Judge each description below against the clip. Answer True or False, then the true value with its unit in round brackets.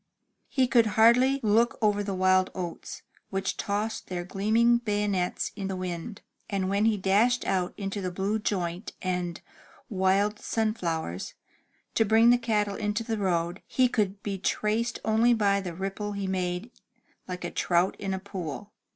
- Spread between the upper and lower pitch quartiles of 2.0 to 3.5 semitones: True (2.9 semitones)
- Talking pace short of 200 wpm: True (160 wpm)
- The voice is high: True (200 Hz)